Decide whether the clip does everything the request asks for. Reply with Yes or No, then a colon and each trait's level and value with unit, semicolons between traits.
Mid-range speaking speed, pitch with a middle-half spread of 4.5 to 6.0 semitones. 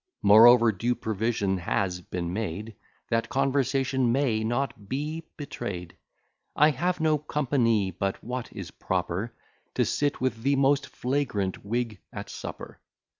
No: slow, 130 wpm; average, 5.2 semitones